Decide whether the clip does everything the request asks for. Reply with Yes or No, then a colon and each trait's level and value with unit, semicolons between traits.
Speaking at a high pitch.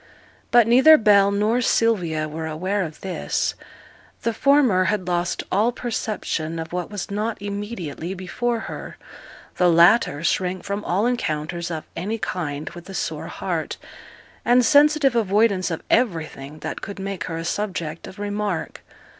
Yes: high, 195 Hz